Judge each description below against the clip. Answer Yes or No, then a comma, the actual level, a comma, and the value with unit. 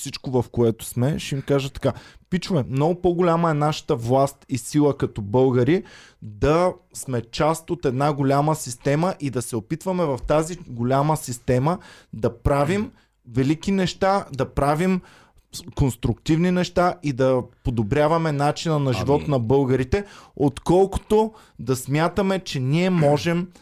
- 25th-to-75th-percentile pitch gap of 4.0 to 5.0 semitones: Yes, average, 4.6 semitones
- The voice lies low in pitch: No, medium, 145 Hz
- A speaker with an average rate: Yes, average, 140 wpm